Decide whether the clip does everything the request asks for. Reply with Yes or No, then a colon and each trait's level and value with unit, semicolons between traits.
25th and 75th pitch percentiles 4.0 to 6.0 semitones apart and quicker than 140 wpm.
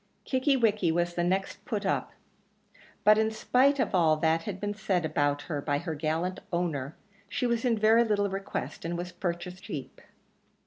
Yes: average, 4.6 semitones; average, 180 wpm